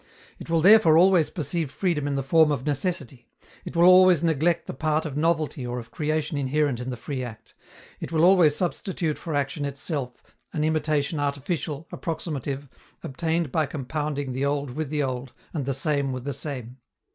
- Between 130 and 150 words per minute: No, average, 180 wpm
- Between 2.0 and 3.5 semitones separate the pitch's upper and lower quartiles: Yes, average, 2.9 semitones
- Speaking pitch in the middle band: Yes, medium, 150 Hz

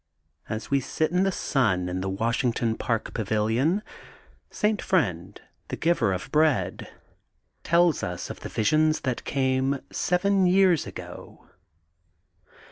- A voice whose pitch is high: No, low, 135 Hz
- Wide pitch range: Yes, wide, 7.9 semitones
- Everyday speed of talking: No, slow, 125 wpm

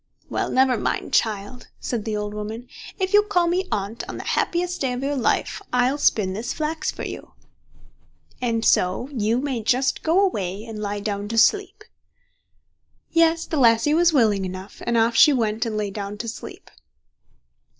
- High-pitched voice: Yes, high, 235 Hz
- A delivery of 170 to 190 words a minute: Yes, average, 180 wpm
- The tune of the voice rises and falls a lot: Yes, wide, 6.0 semitones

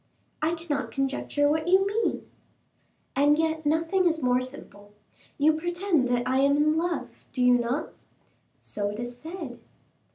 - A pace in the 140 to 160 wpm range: Yes, average, 155 wpm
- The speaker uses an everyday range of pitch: Yes, average, 4.4 semitones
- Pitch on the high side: Yes, very high, 295 Hz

